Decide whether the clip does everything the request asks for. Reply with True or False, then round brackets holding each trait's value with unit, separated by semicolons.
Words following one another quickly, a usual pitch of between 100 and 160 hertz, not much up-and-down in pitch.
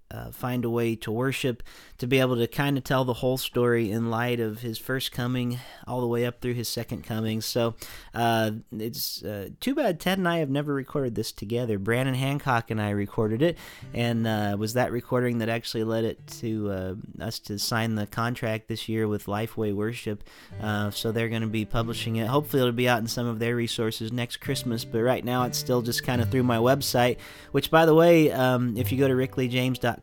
True (220 wpm; 120 Hz; 2.3 semitones)